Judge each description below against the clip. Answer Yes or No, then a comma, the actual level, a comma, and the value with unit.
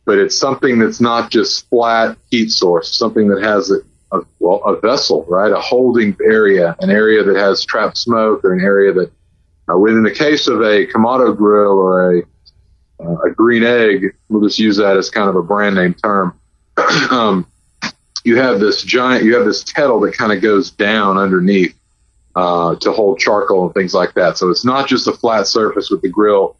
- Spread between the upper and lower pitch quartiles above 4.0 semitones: Yes, average, 4.5 semitones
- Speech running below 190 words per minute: No, average, 200 wpm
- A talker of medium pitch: No, low, 105 Hz